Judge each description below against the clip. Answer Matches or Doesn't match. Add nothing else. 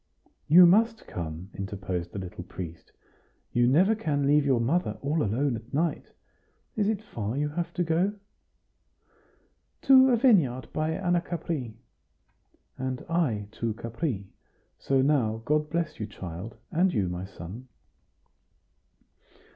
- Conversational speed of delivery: Doesn't match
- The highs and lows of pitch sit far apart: Matches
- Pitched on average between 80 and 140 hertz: Matches